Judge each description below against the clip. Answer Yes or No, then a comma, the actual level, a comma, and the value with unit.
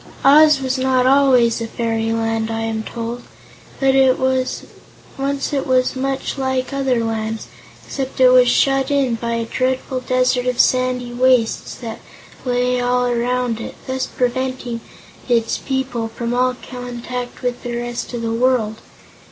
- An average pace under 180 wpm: Yes, average, 145 wpm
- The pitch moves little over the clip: Yes, narrow, 1.9 semitones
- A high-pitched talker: Yes, very high, 250 Hz